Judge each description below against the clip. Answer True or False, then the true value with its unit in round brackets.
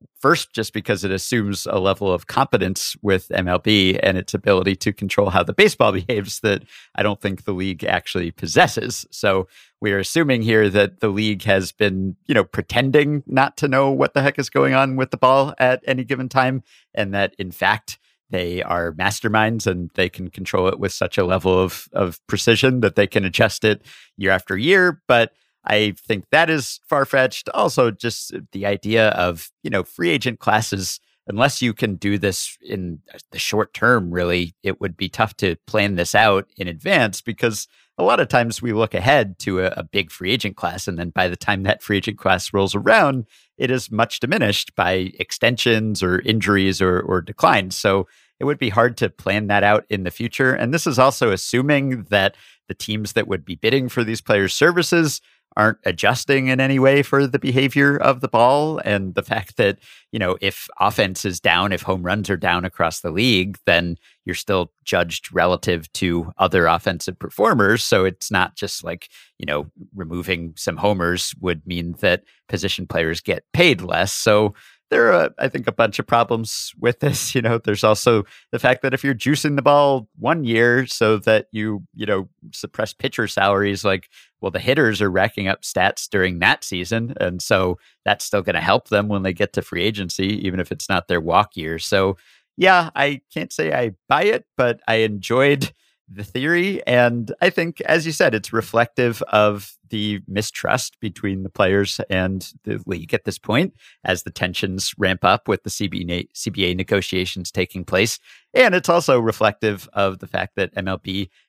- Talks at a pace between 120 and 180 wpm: False (195 wpm)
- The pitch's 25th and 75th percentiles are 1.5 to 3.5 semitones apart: False (4.7 semitones)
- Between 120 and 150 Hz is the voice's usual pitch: False (105 Hz)